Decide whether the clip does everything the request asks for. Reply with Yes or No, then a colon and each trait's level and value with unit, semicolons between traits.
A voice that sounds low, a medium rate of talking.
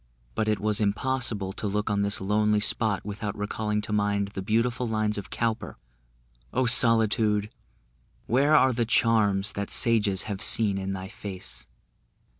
Yes: low, 105 Hz; average, 155 wpm